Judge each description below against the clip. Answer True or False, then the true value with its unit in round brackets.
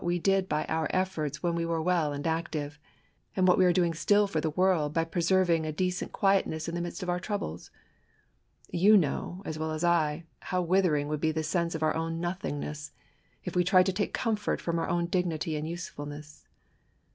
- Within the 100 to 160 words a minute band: False (205 wpm)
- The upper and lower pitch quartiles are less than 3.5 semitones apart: True (2.7 semitones)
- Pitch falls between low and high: True (170 Hz)